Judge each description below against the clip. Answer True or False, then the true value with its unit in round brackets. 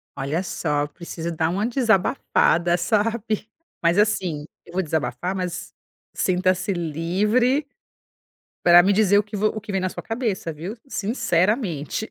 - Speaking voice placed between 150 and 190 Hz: True (185 Hz)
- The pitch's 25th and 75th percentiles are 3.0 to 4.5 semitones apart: True (4.0 semitones)